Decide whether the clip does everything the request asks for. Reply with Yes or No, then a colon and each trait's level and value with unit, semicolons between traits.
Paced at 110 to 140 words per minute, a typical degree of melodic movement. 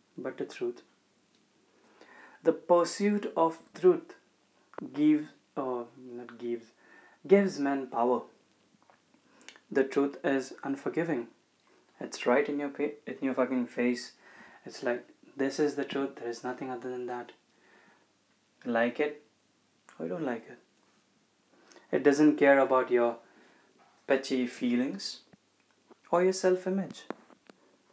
No: average, 120 wpm; wide, 6.8 semitones